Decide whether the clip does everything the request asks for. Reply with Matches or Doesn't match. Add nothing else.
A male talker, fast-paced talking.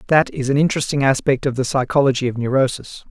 Doesn't match